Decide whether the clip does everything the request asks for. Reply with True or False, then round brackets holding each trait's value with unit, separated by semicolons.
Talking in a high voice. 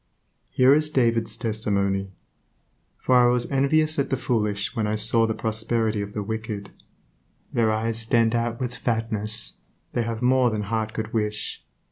False (115 Hz)